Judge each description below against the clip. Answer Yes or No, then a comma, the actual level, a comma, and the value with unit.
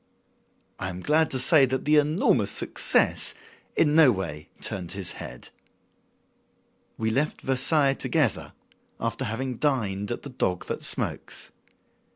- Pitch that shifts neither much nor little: No, wide, 7.1 semitones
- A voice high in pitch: No, low, 130 Hz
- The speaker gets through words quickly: No, slow, 135 wpm